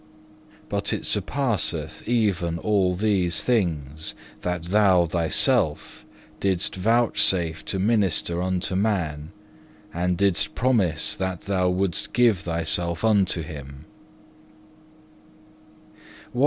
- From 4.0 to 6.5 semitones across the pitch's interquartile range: No, average, 3.3 semitones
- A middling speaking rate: No, slow, 95 wpm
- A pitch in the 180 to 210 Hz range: No, very low, 90 Hz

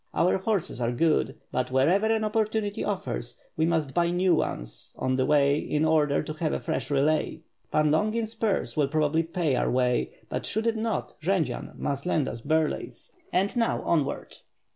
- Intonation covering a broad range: Yes, wide, 5.8 semitones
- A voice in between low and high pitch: Yes, medium, 160 Hz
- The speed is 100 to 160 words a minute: No, average, 180 wpm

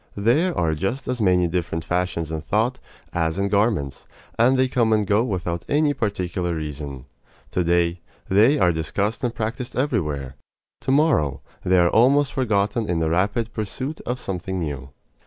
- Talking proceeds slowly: No, average, 165 wpm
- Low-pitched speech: Yes, low, 100 Hz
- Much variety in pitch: Yes, wide, 6.2 semitones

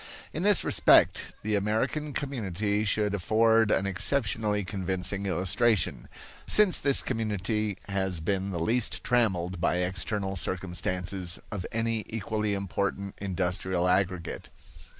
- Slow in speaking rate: Yes, slow, 115 wpm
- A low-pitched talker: Yes, low, 100 Hz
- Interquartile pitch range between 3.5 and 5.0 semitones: No, average, 3.0 semitones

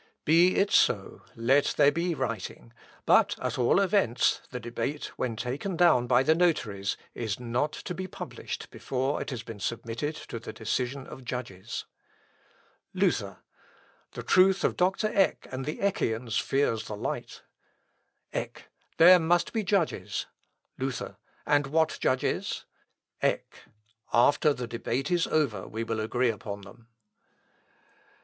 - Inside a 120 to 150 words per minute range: Yes, average, 140 wpm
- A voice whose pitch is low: Yes, low, 130 Hz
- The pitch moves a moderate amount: No, wide, 6.0 semitones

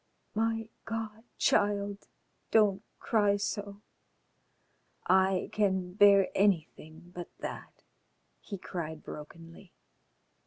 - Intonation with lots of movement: No, narrow, 2.6 semitones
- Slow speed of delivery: Yes, slow, 85 wpm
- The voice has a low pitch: No, high, 200 Hz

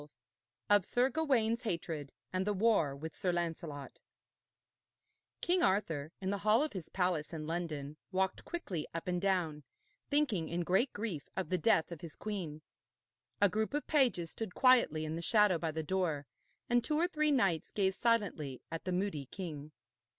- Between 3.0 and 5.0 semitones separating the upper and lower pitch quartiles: No, wide, 5.4 semitones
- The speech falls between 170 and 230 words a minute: Yes, average, 175 wpm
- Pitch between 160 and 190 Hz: Yes, medium, 185 Hz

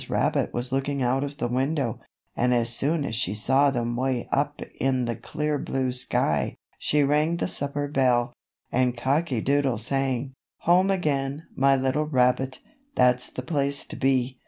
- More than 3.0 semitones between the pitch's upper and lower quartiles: No, narrow, 2.4 semitones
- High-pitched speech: No, low, 135 Hz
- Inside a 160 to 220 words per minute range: Yes, average, 170 wpm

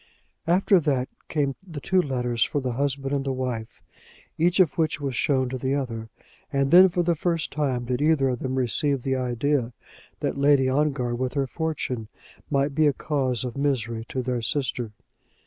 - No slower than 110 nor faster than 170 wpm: No, average, 180 wpm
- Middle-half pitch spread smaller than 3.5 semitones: Yes, average, 2.8 semitones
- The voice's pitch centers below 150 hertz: Yes, low, 135 Hz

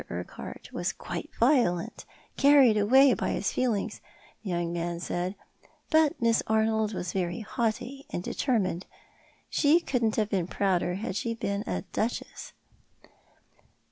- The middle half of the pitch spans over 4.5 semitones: Yes, average, 5.0 semitones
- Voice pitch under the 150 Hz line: No, high, 215 Hz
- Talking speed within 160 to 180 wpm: No, average, 140 wpm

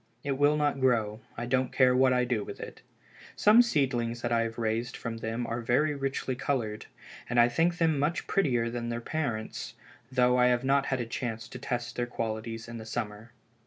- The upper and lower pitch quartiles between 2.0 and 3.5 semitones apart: Yes, average, 2.8 semitones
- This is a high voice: No, low, 120 Hz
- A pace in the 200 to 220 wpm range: Yes, fast, 205 wpm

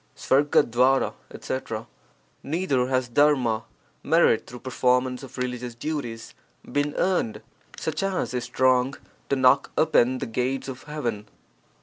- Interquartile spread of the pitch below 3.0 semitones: Yes, narrow, 2.6 semitones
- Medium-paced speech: No, slow, 125 wpm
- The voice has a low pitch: Yes, low, 130 Hz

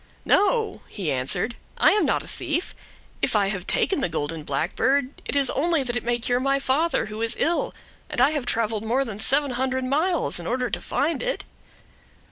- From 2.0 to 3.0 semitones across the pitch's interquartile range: No, average, 4.9 semitones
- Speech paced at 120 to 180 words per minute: No, average, 200 wpm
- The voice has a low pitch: No, very high, 255 Hz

